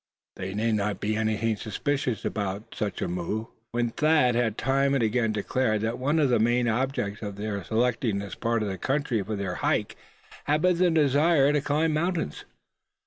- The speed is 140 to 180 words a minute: No, average, 190 wpm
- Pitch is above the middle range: No, low, 115 Hz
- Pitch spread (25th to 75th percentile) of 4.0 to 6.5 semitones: Yes, average, 4.7 semitones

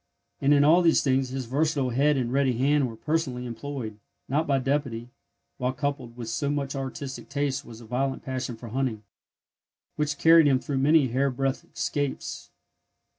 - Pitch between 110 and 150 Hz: Yes, low, 135 Hz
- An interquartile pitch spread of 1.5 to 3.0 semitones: Yes, narrow, 2.4 semitones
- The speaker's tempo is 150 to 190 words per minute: Yes, average, 170 wpm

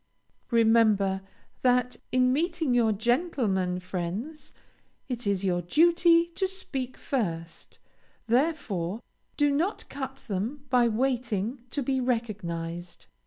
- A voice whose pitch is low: No, high, 240 Hz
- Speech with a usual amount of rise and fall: No, wide, 6.2 semitones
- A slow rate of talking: Yes, slow, 110 wpm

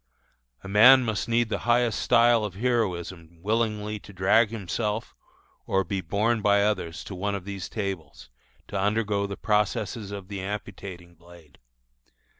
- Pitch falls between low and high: No, low, 100 Hz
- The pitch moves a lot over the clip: No, average, 2.7 semitones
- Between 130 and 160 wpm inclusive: Yes, average, 150 wpm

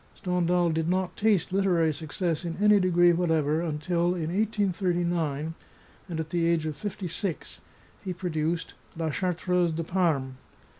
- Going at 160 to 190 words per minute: No, average, 150 wpm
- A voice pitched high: No, medium, 170 Hz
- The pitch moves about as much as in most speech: No, narrow, 2.1 semitones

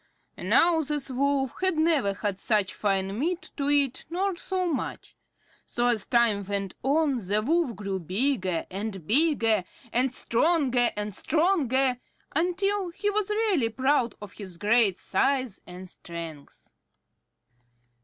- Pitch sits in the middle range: No, very high, 250 Hz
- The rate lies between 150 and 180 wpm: No, slow, 135 wpm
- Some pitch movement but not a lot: No, wide, 7.8 semitones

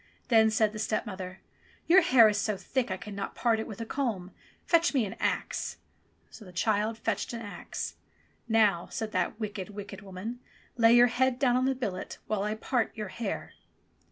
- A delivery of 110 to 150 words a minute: No, average, 190 wpm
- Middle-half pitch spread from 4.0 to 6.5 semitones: No, average, 3.1 semitones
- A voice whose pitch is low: No, high, 220 Hz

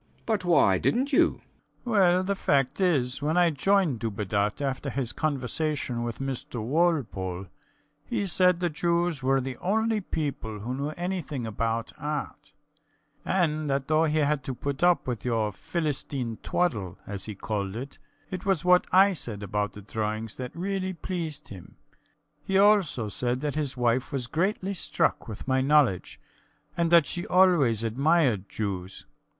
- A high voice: No, medium, 140 Hz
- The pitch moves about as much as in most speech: No, wide, 7.1 semitones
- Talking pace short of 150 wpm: No, average, 165 wpm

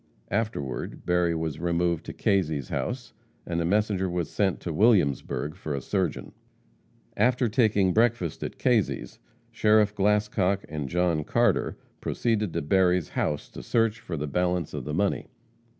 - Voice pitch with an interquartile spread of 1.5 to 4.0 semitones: No, average, 4.6 semitones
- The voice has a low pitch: Yes, very low, 90 Hz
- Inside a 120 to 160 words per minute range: Yes, average, 150 wpm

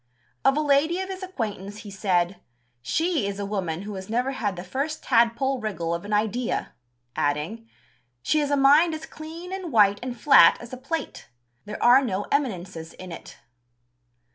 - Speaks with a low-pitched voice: No, high, 230 Hz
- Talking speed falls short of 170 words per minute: No, average, 180 wpm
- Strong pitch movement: Yes, wide, 6.6 semitones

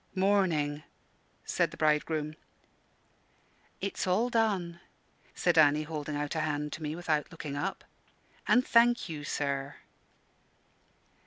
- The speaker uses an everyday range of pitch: Yes, average, 4.0 semitones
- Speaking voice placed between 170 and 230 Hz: No, medium, 155 Hz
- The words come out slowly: Yes, slow, 115 wpm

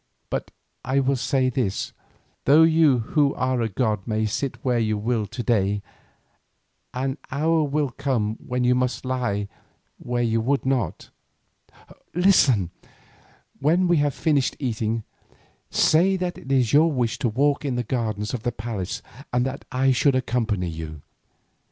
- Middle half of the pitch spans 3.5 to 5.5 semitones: Yes, average, 3.9 semitones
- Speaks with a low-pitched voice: Yes, low, 125 Hz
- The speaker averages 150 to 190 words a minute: Yes, average, 155 wpm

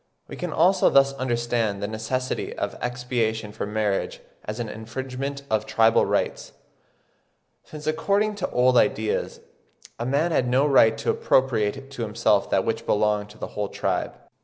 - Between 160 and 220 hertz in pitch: No, low, 120 Hz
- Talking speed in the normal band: Yes, average, 160 wpm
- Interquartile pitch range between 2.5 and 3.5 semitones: No, average, 3.9 semitones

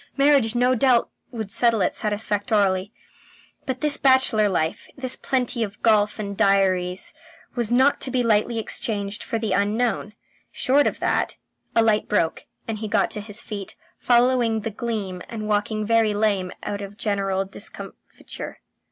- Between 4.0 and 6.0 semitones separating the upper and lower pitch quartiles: No, average, 2.9 semitones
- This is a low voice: No, high, 215 Hz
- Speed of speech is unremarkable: Yes, average, 155 wpm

